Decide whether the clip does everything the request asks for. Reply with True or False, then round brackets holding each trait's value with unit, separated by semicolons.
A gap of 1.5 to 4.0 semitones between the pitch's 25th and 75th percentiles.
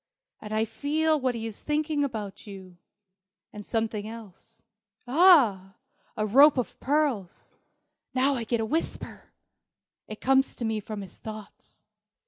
False (4.9 semitones)